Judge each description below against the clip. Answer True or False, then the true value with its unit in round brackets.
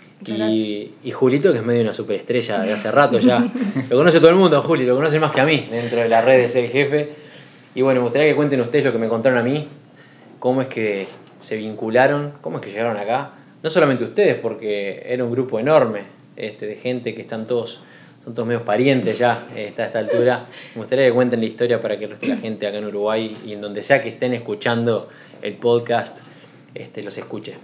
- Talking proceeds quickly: True (225 wpm)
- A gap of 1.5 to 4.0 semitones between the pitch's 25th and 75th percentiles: True (3.4 semitones)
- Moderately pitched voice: False (120 Hz)